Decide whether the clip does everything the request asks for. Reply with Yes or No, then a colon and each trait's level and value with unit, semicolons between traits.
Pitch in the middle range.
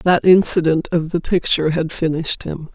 Yes: medium, 165 Hz